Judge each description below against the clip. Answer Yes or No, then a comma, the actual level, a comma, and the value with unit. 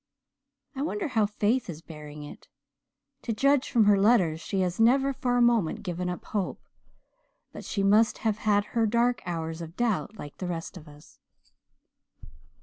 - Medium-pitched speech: No, high, 205 Hz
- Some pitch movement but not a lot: No, wide, 5.7 semitones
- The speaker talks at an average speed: Yes, average, 170 wpm